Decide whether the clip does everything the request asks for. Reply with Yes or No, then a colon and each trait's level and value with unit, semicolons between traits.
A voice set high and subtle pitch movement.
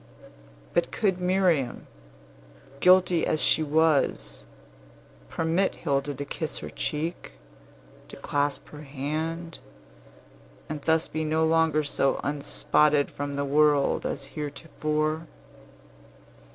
No: medium, 155 Hz; narrow, 2.2 semitones